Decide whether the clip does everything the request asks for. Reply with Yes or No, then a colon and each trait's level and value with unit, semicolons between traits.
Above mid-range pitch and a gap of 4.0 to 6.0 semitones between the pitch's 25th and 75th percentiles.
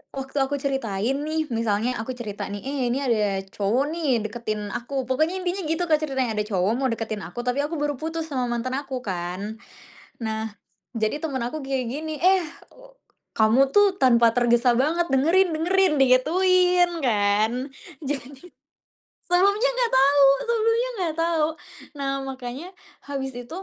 Yes: very high, 270 Hz; wide, 5.5 semitones